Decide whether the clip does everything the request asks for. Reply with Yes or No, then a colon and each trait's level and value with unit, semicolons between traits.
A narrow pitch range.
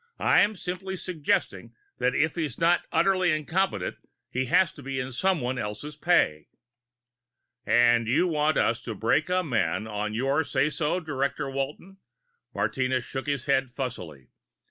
No: average, 5.3 semitones